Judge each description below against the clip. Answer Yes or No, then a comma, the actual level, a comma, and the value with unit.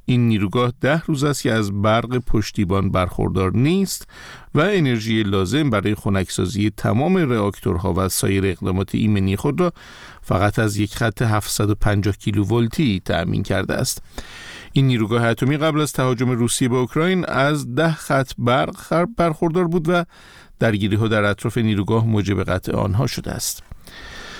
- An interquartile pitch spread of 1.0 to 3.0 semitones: No, average, 5.1 semitones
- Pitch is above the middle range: No, low, 115 Hz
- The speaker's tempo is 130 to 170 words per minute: Yes, average, 150 wpm